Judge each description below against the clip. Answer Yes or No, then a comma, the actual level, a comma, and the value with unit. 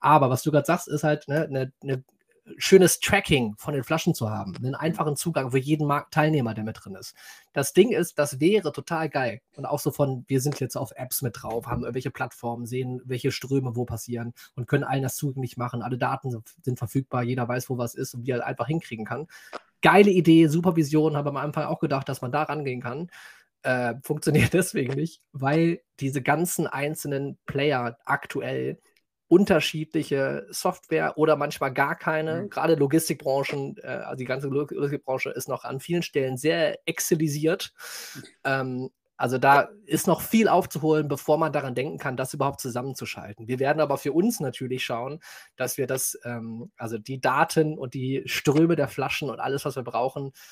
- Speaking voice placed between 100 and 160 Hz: Yes, medium, 140 Hz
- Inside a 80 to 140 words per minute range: No, average, 185 wpm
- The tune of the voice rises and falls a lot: No, average, 3.5 semitones